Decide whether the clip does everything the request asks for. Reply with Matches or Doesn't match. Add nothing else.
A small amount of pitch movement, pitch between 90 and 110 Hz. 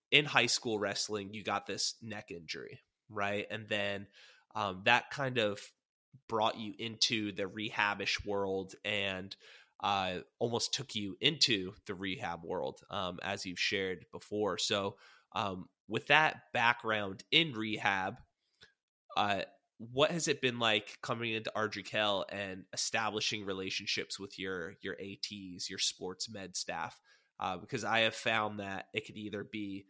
Matches